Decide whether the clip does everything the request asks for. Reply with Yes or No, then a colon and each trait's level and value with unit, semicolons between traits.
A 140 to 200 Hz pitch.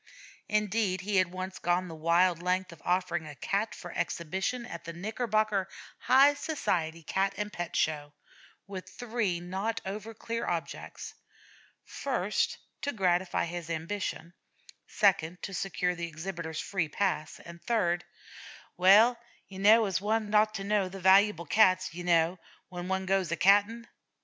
Yes: medium, 185 Hz